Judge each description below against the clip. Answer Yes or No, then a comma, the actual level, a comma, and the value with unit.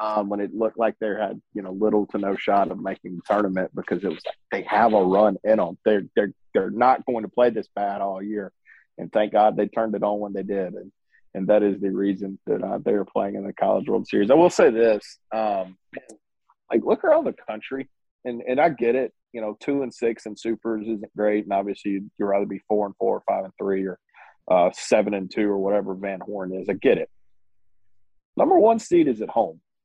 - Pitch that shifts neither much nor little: No, narrow, 1.6 semitones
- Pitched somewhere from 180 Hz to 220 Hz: No, low, 100 Hz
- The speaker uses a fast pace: Yes, fast, 240 wpm